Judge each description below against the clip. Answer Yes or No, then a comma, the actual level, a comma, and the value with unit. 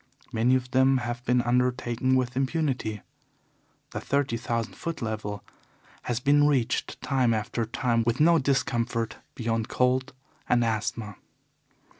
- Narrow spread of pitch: Yes, narrow, 2.2 semitones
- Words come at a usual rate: No, slow, 130 wpm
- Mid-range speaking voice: No, low, 125 Hz